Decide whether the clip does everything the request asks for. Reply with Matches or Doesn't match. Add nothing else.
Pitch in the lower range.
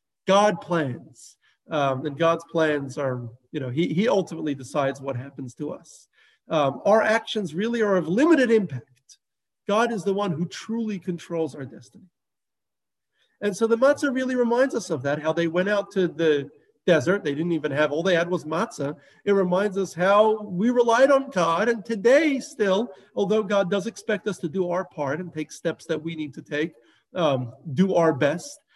Doesn't match